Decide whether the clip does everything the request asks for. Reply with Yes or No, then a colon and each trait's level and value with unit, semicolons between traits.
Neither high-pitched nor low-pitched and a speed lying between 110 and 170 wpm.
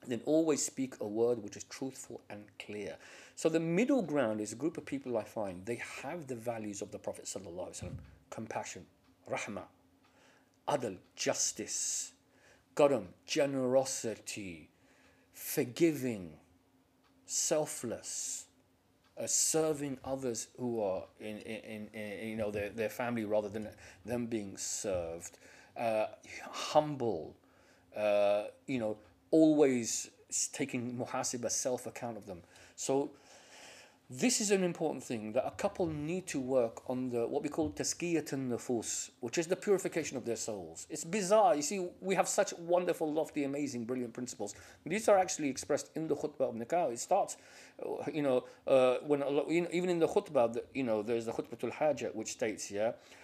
No: low, 130 Hz; average, 160 wpm